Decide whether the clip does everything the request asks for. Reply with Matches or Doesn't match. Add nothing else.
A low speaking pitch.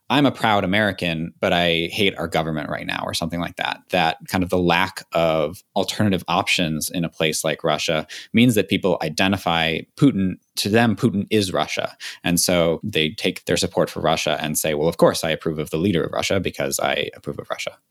Matches